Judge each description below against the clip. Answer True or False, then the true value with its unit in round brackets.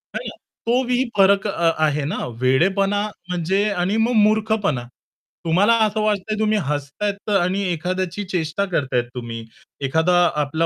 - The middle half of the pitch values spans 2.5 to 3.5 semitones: False (4.7 semitones)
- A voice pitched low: False (185 Hz)